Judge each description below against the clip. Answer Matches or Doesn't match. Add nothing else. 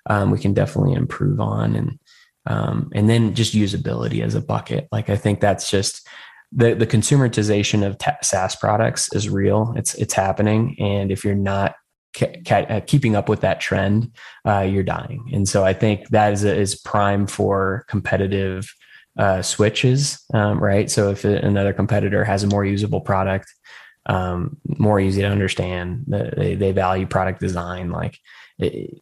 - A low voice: Matches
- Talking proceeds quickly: Doesn't match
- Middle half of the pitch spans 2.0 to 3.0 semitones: Matches